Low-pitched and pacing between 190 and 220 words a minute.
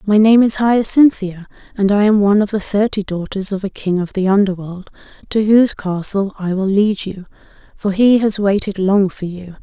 No: high, 200 Hz; average, 200 wpm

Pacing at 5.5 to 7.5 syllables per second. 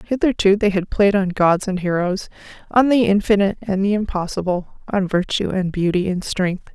No: 5.2 syllables/s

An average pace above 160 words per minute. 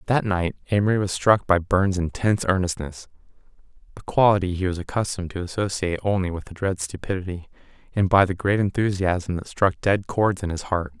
Yes: average, 185 wpm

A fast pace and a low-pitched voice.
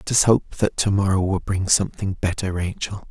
Yes: fast, 210 wpm; very low, 95 Hz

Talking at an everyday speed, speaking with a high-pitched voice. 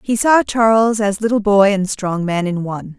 No: fast, 220 wpm; high, 205 Hz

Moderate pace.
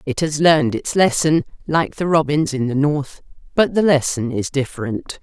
Yes: average, 185 wpm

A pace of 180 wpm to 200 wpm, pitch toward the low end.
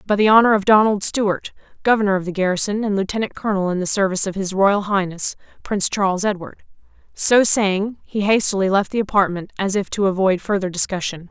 No: average, 190 wpm; high, 195 Hz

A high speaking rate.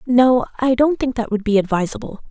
Yes: fast, 210 wpm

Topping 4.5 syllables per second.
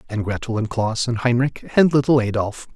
Yes: 5.4 syllables/s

